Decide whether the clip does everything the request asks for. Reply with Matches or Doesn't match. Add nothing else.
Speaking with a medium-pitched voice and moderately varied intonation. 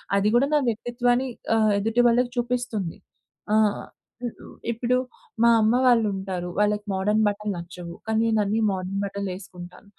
Doesn't match